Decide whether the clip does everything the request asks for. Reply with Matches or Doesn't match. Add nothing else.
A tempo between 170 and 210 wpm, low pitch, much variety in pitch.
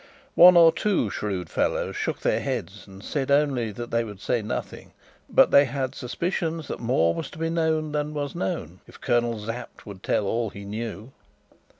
Matches